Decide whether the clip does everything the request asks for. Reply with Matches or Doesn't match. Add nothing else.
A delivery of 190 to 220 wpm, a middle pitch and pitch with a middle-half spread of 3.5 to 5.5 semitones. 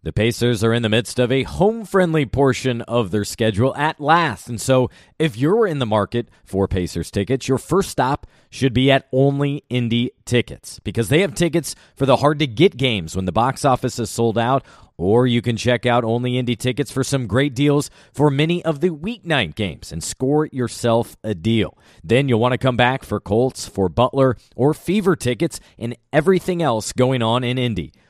Doesn't match